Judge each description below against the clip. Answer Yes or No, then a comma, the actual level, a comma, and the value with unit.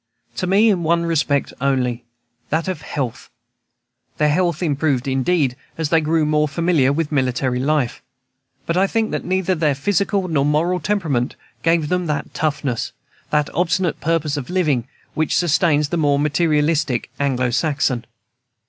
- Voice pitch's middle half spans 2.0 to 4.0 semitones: Yes, average, 3.4 semitones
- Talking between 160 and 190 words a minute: No, average, 150 wpm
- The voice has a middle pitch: Yes, medium, 150 Hz